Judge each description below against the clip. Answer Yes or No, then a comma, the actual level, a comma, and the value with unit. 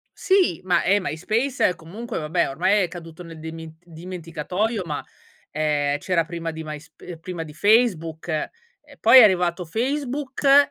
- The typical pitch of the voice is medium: Yes, medium, 175 Hz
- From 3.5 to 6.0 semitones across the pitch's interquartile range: Yes, average, 5.2 semitones